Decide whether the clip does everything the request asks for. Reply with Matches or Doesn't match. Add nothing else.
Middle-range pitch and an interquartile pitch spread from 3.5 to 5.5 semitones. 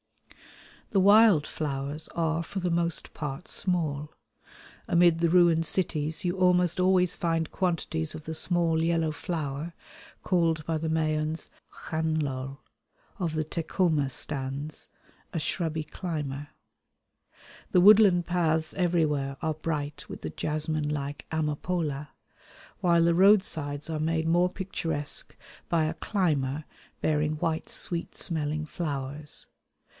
Doesn't match